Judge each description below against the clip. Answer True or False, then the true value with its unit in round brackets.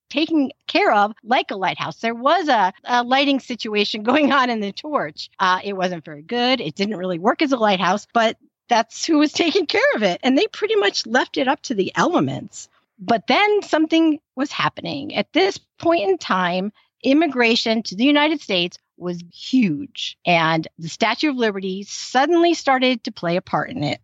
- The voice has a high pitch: True (245 Hz)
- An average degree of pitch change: False (6.9 semitones)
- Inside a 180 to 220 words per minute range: True (190 wpm)